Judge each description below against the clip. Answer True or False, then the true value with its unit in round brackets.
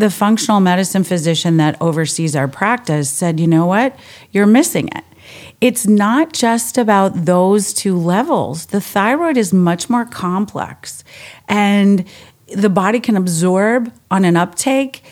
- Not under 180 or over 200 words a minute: False (145 wpm)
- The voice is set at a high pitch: True (200 Hz)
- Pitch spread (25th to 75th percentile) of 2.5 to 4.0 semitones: False (4.6 semitones)